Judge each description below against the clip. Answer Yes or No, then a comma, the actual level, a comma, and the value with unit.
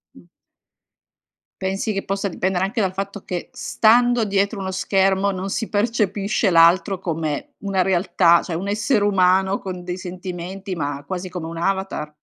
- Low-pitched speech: No, high, 190 Hz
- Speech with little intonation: Yes, narrow, 2.0 semitones